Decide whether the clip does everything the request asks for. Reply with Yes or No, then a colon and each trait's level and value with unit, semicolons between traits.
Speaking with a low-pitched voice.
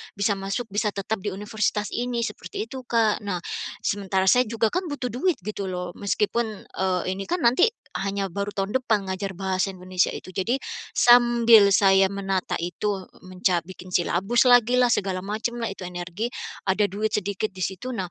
No: high, 200 Hz